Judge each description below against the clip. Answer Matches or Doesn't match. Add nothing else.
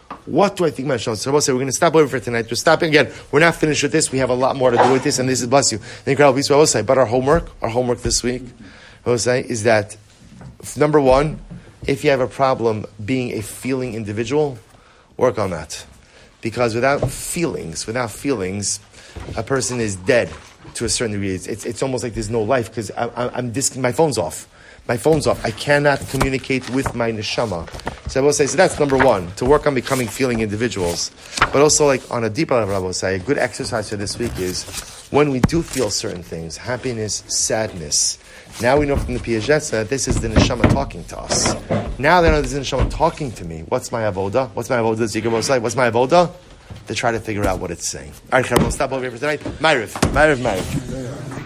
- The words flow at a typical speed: Doesn't match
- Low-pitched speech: Matches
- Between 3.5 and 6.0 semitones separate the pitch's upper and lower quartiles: Matches